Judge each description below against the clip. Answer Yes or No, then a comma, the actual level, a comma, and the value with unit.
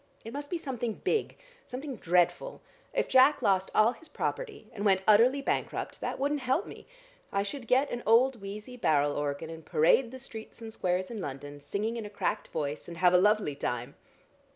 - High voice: Yes, high, 215 Hz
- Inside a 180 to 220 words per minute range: Yes, average, 195 wpm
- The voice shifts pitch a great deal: Yes, wide, 6.5 semitones